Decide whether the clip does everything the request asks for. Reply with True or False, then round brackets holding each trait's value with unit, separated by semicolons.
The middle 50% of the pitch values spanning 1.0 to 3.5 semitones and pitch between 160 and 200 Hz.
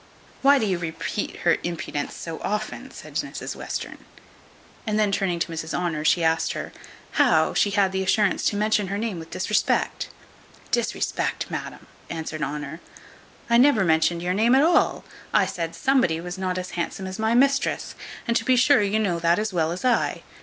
False (4.6 semitones; 190 Hz)